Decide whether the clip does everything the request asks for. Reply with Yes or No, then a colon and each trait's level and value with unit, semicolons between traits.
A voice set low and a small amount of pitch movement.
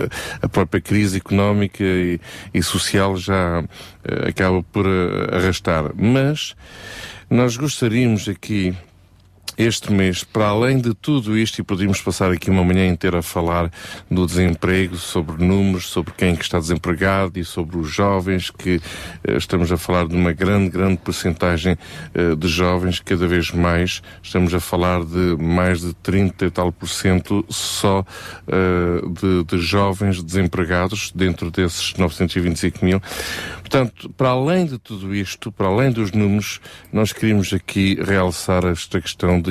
Yes: very low, 95 Hz; narrow, 2.1 semitones